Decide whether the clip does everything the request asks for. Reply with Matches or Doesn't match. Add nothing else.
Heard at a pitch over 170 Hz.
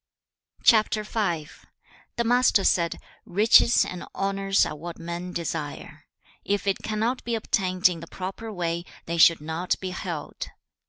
Matches